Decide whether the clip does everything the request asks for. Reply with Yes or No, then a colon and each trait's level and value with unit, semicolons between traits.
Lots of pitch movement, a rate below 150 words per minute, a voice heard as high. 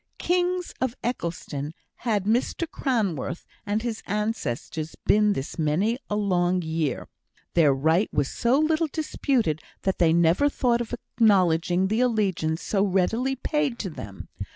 Yes: wide, 6.7 semitones; average, 140 wpm; high, 205 Hz